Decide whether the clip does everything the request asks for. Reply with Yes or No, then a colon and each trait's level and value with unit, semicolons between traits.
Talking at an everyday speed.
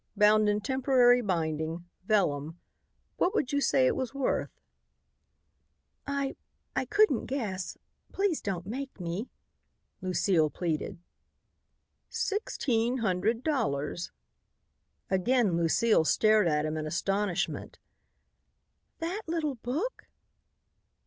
No: slow, 100 wpm